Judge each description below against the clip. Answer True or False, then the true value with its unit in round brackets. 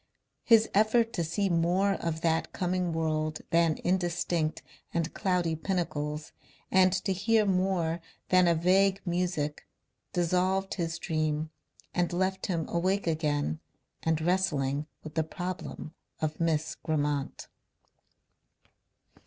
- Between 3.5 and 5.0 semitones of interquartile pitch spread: False (2.9 semitones)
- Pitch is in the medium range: True (170 Hz)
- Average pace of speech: False (120 wpm)